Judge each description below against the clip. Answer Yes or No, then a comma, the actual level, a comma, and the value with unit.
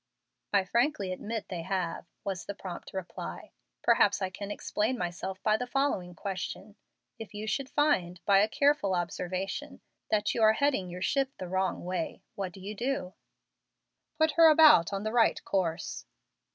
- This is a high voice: Yes, high, 200 Hz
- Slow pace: No, average, 165 wpm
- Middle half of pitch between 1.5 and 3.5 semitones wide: No, average, 4.5 semitones